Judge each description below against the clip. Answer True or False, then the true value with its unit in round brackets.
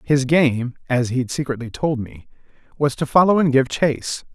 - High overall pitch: False (135 Hz)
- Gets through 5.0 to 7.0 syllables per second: False (4.8 syllables/s)